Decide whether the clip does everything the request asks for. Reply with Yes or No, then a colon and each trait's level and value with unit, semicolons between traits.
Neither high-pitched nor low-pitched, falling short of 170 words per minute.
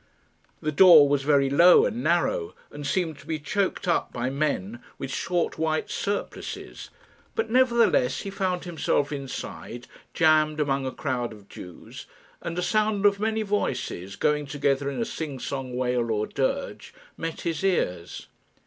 Yes: medium, 150 Hz; average, 160 wpm